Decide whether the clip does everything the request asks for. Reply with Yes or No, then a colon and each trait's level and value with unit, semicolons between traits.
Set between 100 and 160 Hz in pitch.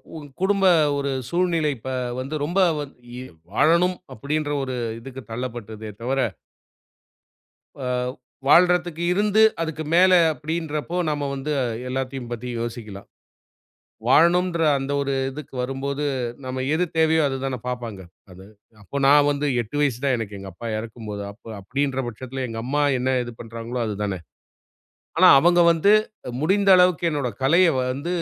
Yes: medium, 140 Hz